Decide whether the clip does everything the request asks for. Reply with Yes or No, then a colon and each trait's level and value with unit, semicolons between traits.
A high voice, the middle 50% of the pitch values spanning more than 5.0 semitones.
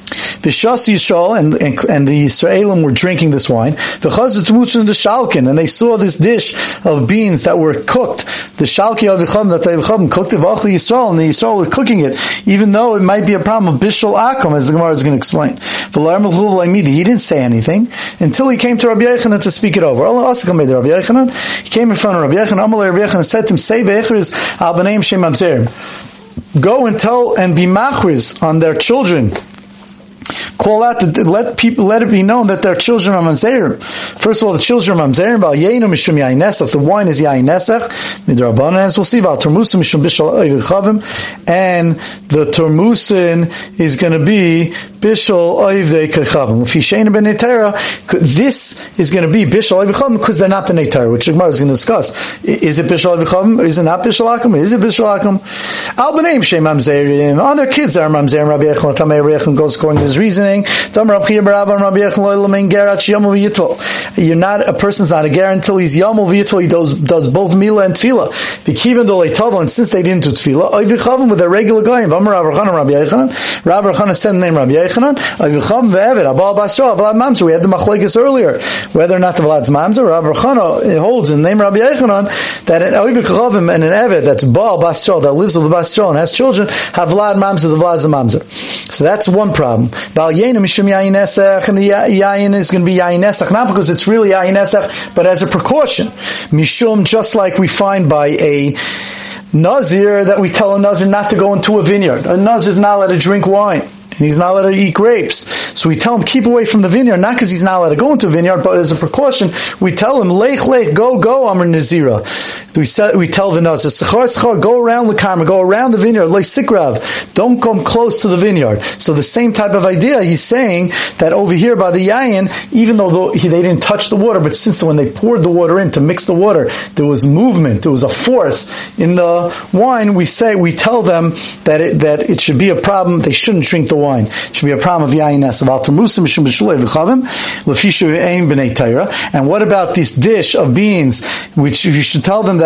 No: high, 195 Hz; average, 4.7 semitones